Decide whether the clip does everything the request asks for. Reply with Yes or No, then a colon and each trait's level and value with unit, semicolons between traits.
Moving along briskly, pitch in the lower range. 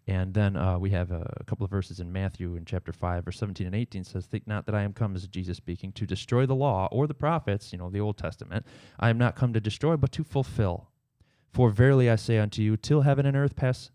Yes: fast, 260 wpm; low, 105 Hz